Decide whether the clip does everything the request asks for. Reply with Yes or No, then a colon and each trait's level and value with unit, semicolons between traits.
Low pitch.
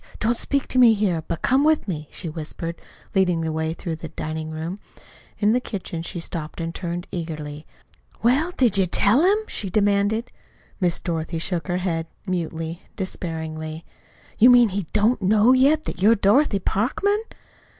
No: medium, 185 Hz